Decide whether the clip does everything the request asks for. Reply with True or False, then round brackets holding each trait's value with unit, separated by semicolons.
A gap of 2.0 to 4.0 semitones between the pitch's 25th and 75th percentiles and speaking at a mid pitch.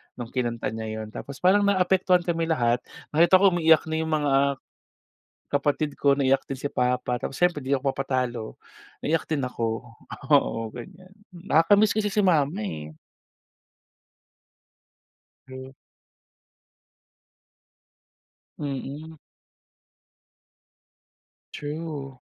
False (4.7 semitones; 145 Hz)